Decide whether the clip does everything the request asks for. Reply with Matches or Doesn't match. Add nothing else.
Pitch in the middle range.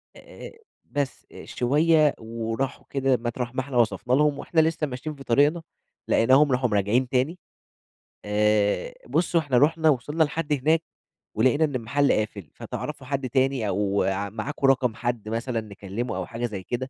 Doesn't match